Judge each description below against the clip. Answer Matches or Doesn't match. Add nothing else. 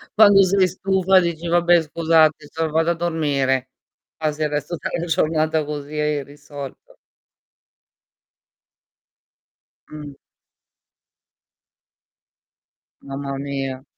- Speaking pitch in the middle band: Matches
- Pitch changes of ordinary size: Matches